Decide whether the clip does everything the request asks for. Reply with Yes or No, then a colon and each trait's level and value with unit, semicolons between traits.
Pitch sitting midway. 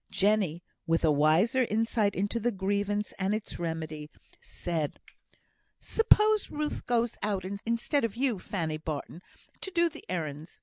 No: high, 200 Hz